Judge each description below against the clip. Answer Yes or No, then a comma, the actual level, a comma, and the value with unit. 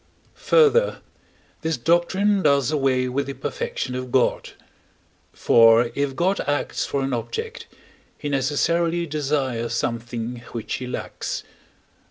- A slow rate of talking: Yes, slow, 120 wpm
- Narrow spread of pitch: No, average, 5.1 semitones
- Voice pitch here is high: No, medium, 140 Hz